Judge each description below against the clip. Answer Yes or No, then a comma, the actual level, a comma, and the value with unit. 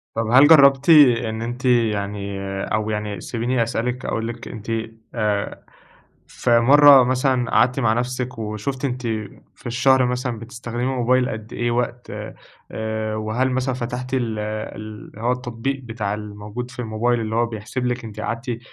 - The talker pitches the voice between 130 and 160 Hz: No, low, 120 Hz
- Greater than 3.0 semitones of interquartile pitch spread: No, narrow, 2.5 semitones